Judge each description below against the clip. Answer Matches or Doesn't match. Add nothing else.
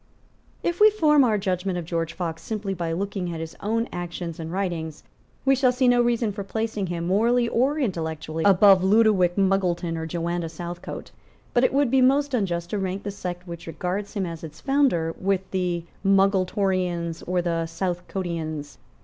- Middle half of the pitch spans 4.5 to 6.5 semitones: Doesn't match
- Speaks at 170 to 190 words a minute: Matches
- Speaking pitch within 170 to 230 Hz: Matches